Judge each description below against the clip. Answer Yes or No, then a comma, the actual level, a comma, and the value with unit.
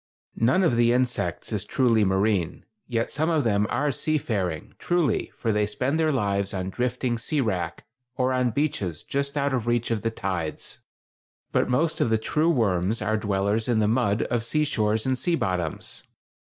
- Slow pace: No, average, 185 wpm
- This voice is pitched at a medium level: No, low, 115 Hz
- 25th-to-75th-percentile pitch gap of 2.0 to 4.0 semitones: No, average, 4.4 semitones